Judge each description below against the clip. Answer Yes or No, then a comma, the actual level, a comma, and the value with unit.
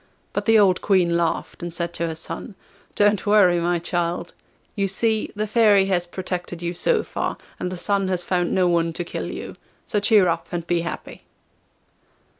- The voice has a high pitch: No, medium, 180 Hz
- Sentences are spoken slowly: No, average, 190 wpm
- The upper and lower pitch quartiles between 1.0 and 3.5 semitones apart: Yes, average, 2.9 semitones